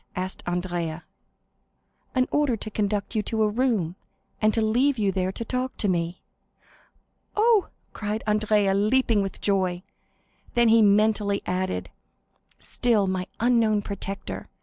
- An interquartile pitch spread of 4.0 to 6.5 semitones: No, average, 3.2 semitones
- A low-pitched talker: No, high, 210 Hz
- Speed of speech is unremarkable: No, slow, 130 wpm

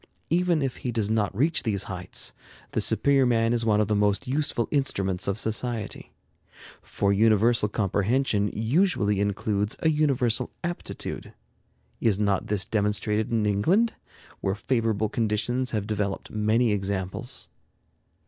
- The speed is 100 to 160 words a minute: Yes, slow, 135 wpm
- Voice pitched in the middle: No, low, 110 Hz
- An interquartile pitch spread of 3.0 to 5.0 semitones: Yes, average, 3.4 semitones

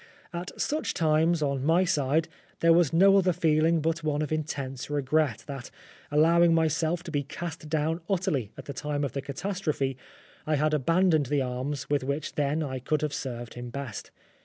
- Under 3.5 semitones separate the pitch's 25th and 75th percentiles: Yes, average, 3.0 semitones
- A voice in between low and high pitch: Yes, medium, 155 Hz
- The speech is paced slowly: No, average, 185 wpm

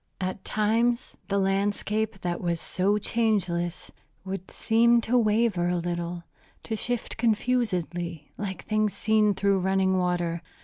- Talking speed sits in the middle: No, slow, 130 wpm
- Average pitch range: Yes, average, 3.7 semitones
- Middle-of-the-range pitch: No, high, 195 Hz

